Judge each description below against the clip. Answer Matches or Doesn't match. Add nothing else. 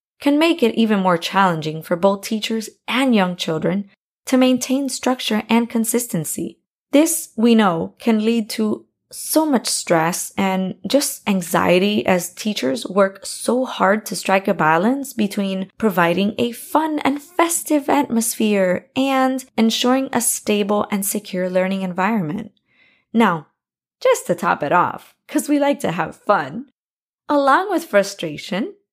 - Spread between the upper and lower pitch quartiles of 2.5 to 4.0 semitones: Doesn't match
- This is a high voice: Matches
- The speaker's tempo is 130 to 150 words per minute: Matches